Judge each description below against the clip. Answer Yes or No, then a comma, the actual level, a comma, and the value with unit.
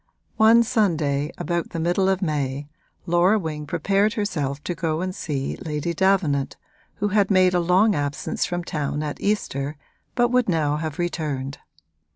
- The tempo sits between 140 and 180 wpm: Yes, average, 160 wpm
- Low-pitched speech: No, medium, 170 Hz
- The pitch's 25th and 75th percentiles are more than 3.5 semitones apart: Yes, average, 4.7 semitones